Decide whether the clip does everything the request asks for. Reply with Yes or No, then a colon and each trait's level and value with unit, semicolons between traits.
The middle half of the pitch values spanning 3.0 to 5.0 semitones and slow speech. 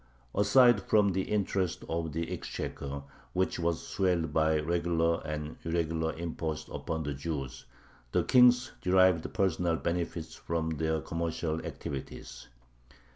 No: narrow, 2.6 semitones; slow, 125 wpm